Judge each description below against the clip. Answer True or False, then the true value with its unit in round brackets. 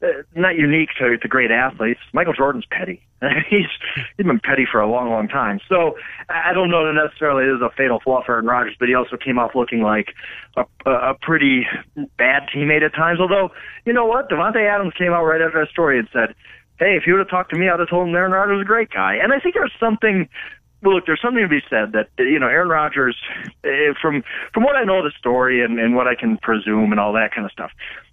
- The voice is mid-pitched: True (155 Hz)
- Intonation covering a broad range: True (7.1 semitones)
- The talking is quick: True (245 wpm)